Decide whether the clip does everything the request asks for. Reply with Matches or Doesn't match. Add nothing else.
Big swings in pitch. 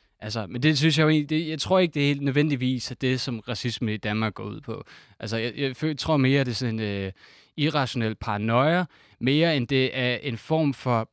Doesn't match